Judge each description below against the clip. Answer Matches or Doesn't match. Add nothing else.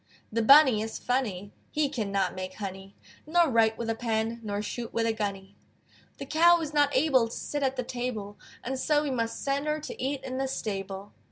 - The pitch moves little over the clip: Doesn't match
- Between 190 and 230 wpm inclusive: Matches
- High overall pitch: Matches